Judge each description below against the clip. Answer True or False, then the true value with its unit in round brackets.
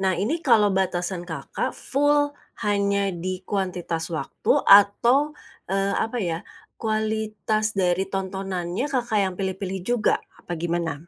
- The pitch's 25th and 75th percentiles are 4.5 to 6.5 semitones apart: False (3.0 semitones)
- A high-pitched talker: True (195 Hz)